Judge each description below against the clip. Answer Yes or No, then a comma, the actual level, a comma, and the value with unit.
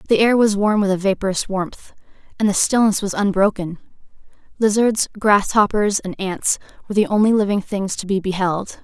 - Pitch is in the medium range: No, high, 200 Hz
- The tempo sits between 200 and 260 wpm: No, average, 170 wpm